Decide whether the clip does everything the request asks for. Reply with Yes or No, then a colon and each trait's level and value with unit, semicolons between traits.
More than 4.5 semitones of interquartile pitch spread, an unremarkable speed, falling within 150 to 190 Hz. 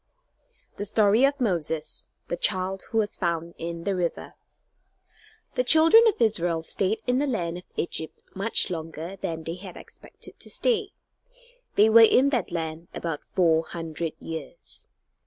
Yes: average, 5.2 semitones; average, 155 wpm; medium, 185 Hz